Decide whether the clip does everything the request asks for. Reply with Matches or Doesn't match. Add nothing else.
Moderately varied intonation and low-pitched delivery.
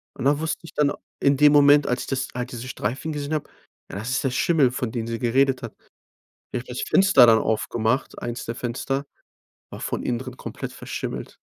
Matches